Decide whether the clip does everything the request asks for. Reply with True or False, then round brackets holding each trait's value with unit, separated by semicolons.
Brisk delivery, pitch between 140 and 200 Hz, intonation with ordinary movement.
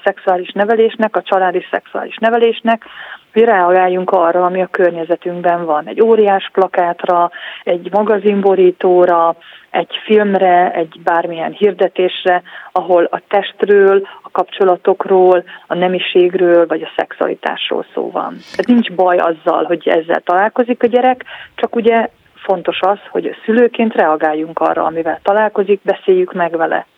False (125 wpm; 185 Hz; 3.5 semitones)